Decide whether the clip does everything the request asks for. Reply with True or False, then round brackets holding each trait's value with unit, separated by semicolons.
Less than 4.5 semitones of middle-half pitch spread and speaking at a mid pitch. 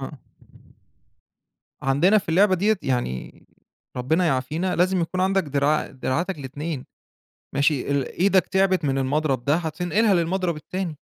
False (5.1 semitones; 160 Hz)